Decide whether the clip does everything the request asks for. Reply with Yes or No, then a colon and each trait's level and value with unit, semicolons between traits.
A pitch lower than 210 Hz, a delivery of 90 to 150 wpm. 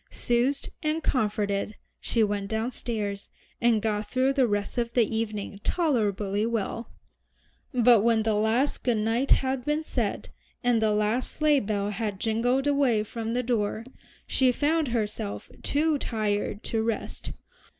No: high, 225 Hz; average, 145 wpm